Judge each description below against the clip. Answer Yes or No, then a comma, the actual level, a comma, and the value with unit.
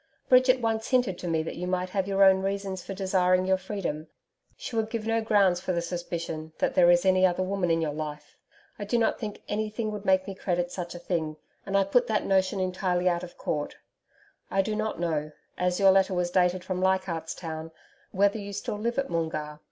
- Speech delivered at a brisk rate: Yes, fast, 220 wpm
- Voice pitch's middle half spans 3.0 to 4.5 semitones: No, narrow, 2.5 semitones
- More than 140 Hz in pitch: Yes, medium, 185 Hz